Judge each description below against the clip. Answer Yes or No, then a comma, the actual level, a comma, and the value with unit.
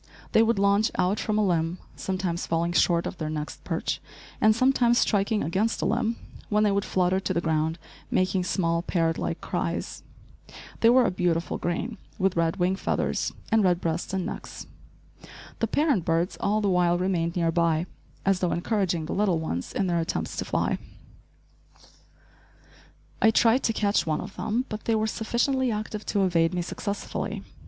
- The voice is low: No, high, 190 Hz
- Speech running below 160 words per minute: No, average, 180 wpm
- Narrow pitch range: No, average, 4.0 semitones